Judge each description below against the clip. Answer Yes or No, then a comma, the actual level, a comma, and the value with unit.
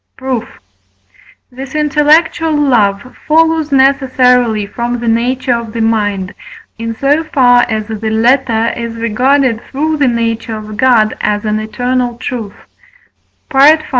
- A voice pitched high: Yes, high, 245 Hz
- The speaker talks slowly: Yes, slow, 130 wpm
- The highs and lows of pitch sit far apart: No, average, 3.5 semitones